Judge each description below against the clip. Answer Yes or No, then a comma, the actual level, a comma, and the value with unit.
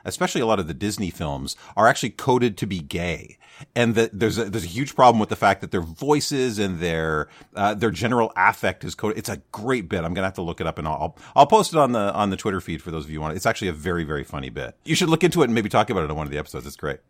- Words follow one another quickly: Yes, fast, 310 wpm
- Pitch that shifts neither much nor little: No, wide, 6.1 semitones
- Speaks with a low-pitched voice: Yes, low, 100 Hz